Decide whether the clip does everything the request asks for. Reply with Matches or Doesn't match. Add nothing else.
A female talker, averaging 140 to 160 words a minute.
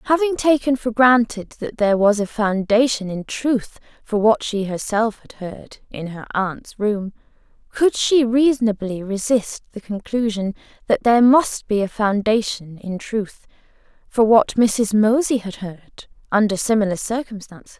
Matches